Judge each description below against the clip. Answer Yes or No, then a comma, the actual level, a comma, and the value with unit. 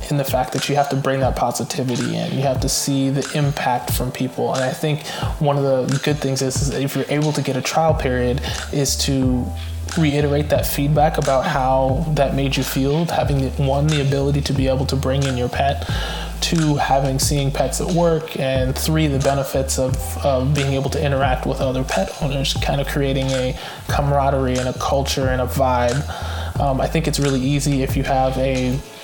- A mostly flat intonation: Yes, narrow, 1.8 semitones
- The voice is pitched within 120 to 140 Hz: Yes, low, 135 Hz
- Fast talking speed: Yes, fast, 210 wpm